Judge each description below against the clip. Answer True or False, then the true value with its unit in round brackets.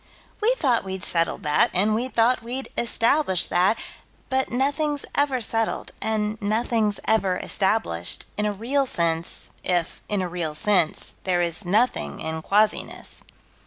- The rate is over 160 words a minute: False (145 wpm)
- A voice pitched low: False (210 Hz)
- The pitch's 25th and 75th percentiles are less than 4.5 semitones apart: False (5.2 semitones)